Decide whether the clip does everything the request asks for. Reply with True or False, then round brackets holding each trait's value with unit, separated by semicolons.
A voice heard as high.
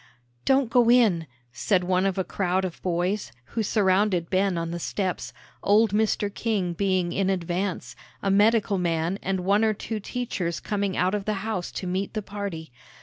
True (195 Hz)